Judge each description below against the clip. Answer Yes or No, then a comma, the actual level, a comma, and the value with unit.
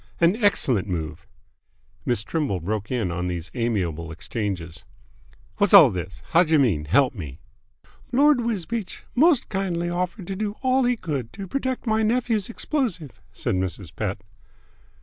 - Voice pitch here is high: No, medium, 145 Hz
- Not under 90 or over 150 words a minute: Yes, average, 140 wpm